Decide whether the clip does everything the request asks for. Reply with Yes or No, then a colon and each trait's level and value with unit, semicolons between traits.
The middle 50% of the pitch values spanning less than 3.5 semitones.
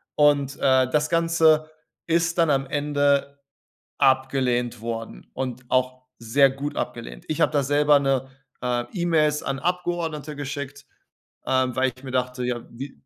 Yes: average, 2.7 semitones